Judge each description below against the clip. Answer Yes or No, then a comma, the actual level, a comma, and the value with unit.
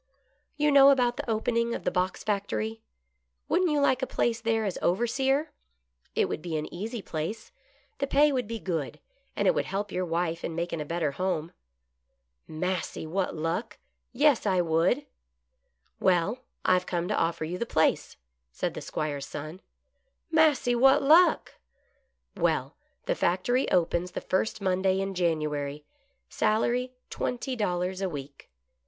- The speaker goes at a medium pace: Yes, average, 165 wpm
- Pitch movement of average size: No, wide, 6.4 semitones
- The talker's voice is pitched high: Yes, high, 195 Hz